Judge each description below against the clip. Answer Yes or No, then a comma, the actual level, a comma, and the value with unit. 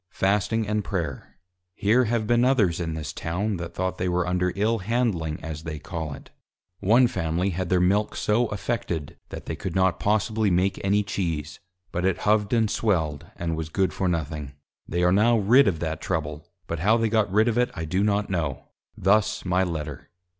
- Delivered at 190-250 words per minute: Yes, average, 200 wpm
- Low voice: Yes, very low, 95 Hz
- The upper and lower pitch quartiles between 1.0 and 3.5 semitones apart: No, average, 4.4 semitones